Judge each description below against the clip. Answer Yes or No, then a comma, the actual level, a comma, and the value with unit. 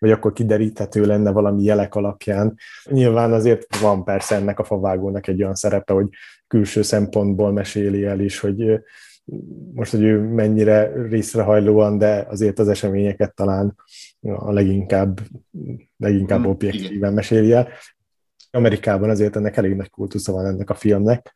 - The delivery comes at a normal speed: Yes, average, 140 wpm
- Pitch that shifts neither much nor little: No, narrow, 1.3 semitones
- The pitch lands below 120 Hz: Yes, low, 105 Hz